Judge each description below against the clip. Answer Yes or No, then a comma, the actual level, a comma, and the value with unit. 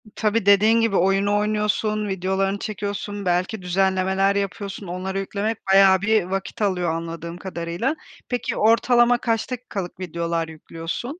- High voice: Yes, high, 195 Hz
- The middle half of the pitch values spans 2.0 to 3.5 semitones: Yes, average, 2.7 semitones